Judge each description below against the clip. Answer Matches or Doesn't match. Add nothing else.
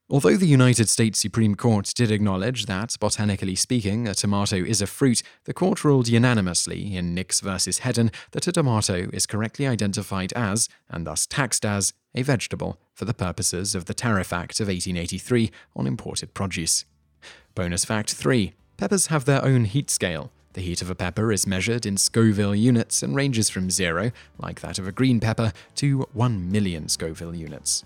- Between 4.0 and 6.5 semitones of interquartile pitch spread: Matches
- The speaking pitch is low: Matches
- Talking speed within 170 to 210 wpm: Matches